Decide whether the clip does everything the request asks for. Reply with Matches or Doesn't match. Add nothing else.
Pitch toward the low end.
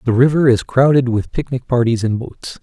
Matches